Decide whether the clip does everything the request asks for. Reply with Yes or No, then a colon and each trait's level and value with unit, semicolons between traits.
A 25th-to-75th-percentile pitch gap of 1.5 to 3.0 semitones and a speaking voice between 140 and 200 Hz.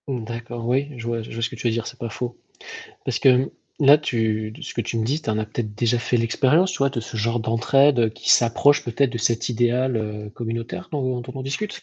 No: narrow, 2.6 semitones; low, 120 Hz